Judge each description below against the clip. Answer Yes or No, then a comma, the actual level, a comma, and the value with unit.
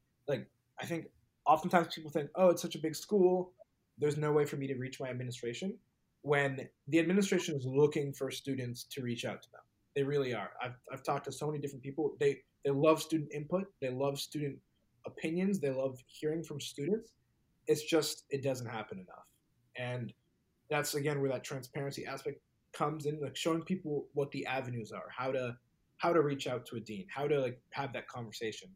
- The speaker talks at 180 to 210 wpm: Yes, average, 200 wpm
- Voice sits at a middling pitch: Yes, medium, 145 Hz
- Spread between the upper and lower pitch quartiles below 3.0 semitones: No, average, 3.3 semitones